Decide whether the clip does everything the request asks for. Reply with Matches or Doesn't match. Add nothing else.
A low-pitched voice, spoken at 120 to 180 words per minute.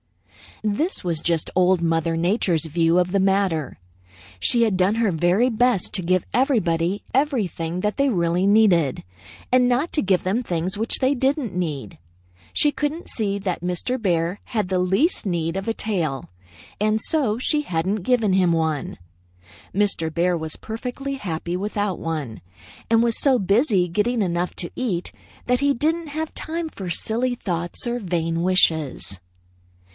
Doesn't match